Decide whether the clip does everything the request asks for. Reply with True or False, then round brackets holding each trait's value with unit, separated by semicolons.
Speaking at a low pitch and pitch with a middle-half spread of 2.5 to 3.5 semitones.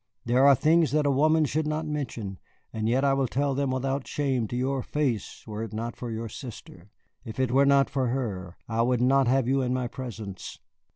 True (130 Hz; 3.1 semitones)